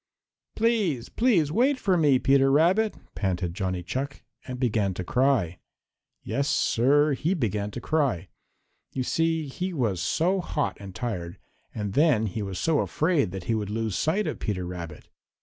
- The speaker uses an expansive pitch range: Yes, wide, 8.2 semitones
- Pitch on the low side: Yes, low, 130 Hz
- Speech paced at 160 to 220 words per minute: Yes, average, 165 wpm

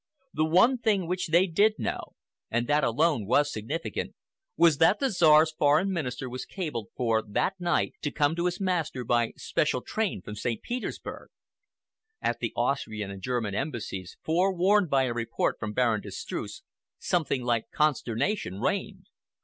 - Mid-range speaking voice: Yes, medium, 150 Hz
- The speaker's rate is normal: Yes, average, 165 wpm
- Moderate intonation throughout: No, wide, 7.0 semitones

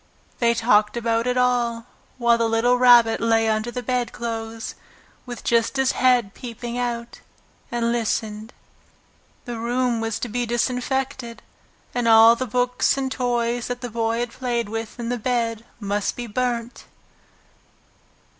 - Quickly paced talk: No, average, 145 wpm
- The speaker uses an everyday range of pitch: No, narrow, 1.5 semitones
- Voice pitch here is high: Yes, high, 235 Hz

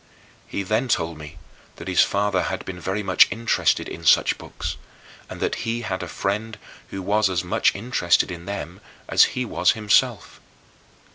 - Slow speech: No, average, 170 wpm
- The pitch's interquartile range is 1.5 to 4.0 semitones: Yes, average, 3.4 semitones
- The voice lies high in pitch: No, very low, 95 Hz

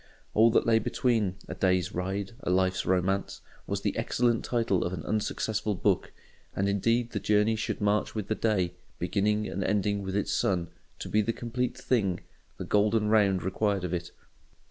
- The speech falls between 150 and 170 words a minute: No, average, 180 wpm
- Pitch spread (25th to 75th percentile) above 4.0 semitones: No, average, 2.8 semitones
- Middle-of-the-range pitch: No, low, 100 Hz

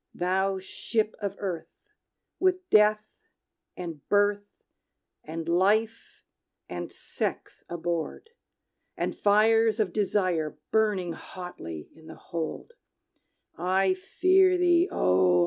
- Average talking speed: No, slow, 100 wpm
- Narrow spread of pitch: No, average, 4.2 semitones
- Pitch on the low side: No, high, 195 Hz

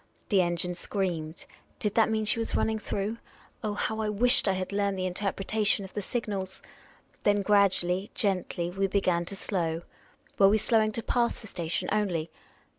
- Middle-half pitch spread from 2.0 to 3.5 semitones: Yes, average, 2.8 semitones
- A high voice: Yes, high, 200 Hz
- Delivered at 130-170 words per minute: No, average, 180 wpm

